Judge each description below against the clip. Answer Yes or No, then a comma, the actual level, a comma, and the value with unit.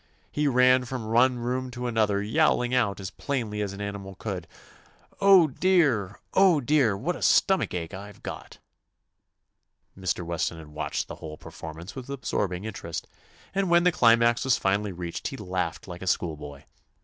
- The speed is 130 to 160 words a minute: No, average, 180 wpm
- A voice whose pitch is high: No, low, 110 Hz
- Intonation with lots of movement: Yes, wide, 5.7 semitones